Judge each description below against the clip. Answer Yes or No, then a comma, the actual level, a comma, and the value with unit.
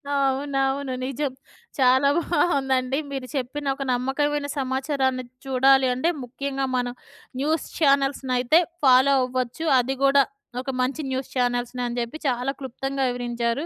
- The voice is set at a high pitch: Yes, very high, 270 Hz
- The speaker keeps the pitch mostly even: Yes, narrow, 1.6 semitones